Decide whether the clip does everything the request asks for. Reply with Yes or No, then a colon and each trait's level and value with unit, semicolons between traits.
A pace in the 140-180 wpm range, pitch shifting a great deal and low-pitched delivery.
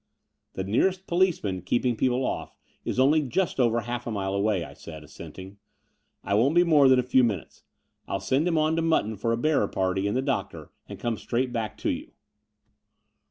No: fast, 205 wpm; wide, 6.0 semitones; low, 120 Hz